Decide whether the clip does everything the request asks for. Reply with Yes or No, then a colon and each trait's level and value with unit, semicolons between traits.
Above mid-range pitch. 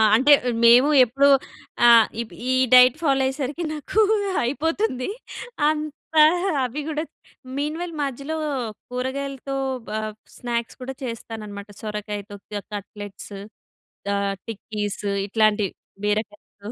Yes: very high, 250 Hz